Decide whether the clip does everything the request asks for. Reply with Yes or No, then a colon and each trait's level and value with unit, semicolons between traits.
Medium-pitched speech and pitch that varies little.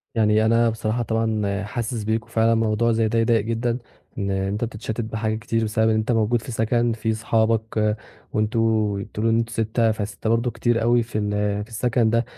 No: low, 110 Hz; narrow, 1.2 semitones